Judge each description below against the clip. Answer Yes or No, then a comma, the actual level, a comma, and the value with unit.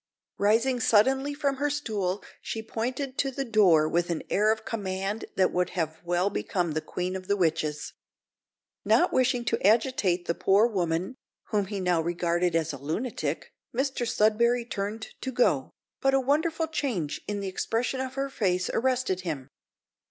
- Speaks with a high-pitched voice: Yes, high, 210 Hz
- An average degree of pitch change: No, wide, 6.2 semitones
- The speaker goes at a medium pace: Yes, average, 165 wpm